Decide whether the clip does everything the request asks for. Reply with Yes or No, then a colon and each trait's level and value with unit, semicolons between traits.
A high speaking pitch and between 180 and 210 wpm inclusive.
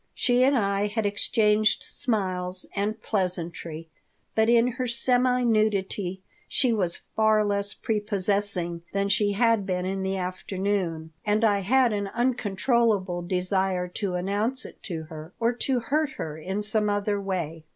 No: high, 205 Hz; average, 150 wpm